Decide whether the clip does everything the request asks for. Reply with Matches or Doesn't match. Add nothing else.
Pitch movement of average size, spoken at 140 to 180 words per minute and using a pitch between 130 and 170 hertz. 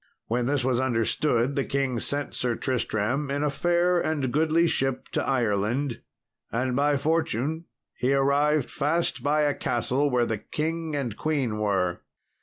Matches